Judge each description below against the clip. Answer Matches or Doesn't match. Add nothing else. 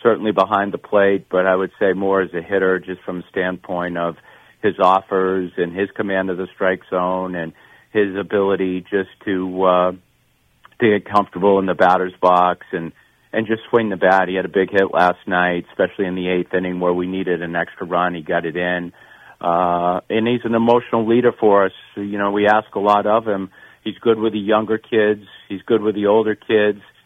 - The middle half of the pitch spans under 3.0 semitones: Matches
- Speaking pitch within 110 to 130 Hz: Doesn't match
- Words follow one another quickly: Matches